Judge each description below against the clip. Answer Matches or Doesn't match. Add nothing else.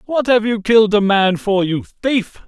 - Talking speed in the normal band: Doesn't match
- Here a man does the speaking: Matches